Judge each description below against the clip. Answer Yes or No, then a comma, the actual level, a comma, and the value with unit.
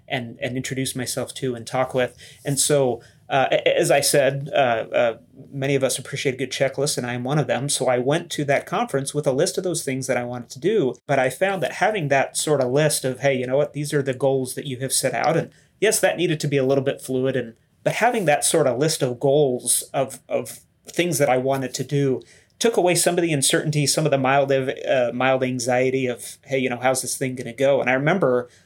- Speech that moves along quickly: Yes, fast, 255 wpm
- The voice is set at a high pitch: No, low, 135 Hz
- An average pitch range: No, narrow, 2.2 semitones